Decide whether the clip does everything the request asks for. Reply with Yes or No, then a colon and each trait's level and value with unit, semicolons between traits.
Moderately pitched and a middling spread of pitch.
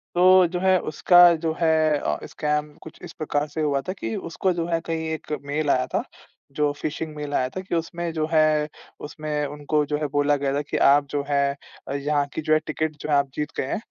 No: medium, 150 Hz; narrow, 1.7 semitones